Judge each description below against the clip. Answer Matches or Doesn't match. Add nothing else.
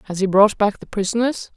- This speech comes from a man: Doesn't match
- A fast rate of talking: Matches